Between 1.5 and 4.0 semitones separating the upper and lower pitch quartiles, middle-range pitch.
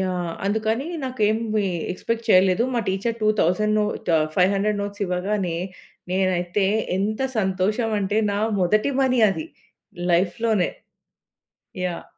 No: average, 2.9 semitones; high, 205 Hz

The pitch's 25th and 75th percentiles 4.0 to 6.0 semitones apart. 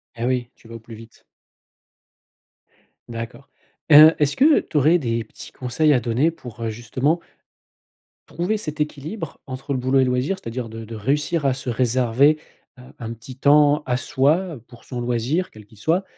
Yes: average, 4.4 semitones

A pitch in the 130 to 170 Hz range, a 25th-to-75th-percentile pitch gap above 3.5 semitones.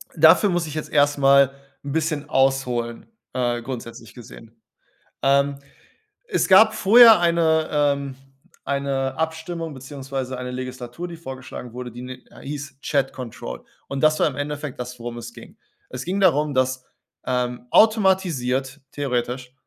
Yes: medium, 140 Hz; average, 3.9 semitones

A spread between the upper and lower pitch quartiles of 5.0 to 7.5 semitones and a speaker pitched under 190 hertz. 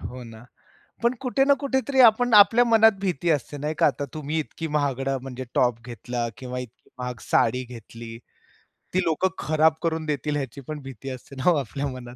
Yes: average, 5.3 semitones; medium, 140 Hz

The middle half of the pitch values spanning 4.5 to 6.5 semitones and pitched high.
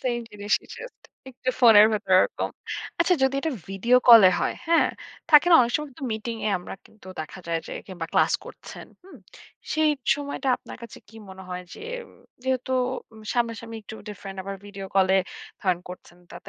Yes: average, 5.2 semitones; high, 225 Hz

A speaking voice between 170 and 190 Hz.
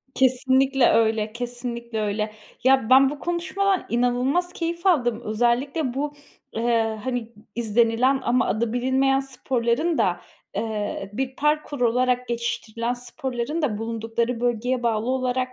No: high, 245 Hz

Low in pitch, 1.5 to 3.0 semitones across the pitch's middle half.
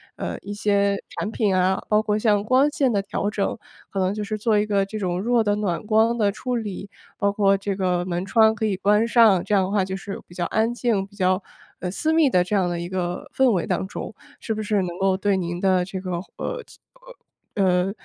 No: high, 200 Hz; narrow, 2.5 semitones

